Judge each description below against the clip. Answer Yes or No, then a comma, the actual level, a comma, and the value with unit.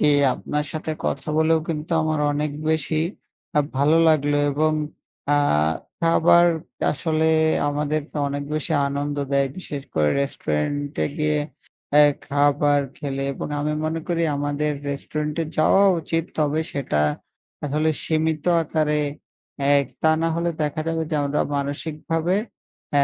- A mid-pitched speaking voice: Yes, medium, 150 Hz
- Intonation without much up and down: Yes, narrow, 1.7 semitones